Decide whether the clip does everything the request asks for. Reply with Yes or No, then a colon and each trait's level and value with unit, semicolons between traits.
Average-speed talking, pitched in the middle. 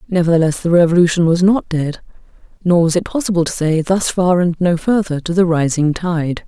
Yes: average, 195 wpm; medium, 170 Hz